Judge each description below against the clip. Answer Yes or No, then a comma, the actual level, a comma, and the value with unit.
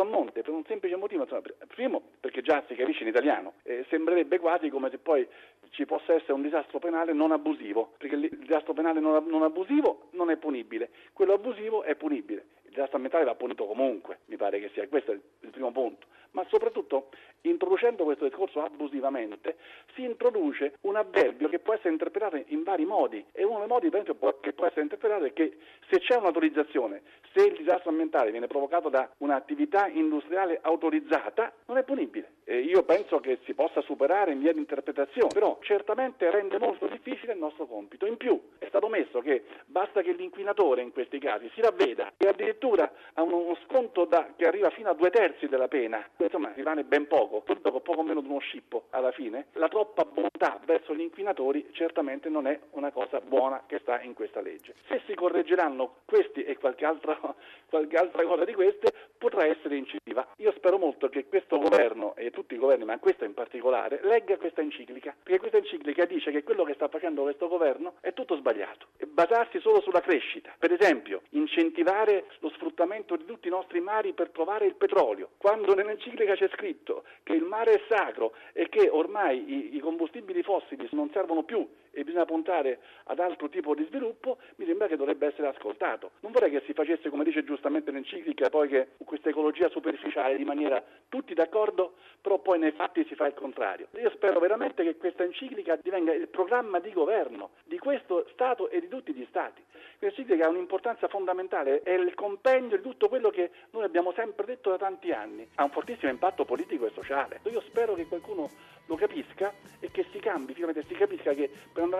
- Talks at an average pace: No, fast, 190 wpm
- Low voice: No, high, 195 Hz